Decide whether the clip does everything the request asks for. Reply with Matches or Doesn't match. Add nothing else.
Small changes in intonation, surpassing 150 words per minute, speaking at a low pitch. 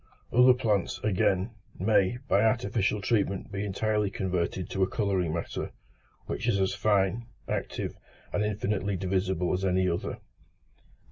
Doesn't match